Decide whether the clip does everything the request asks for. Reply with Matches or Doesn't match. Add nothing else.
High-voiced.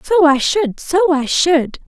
Matches